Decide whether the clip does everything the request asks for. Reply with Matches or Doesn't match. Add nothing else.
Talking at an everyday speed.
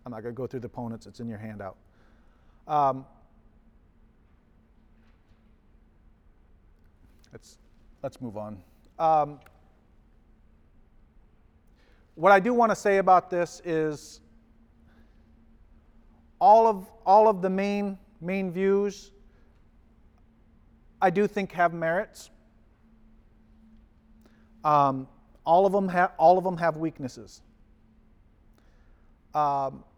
Doesn't match